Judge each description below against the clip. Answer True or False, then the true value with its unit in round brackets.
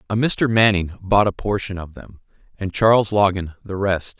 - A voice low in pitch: True (100 Hz)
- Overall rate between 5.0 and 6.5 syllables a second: False (4.8 syllables/s)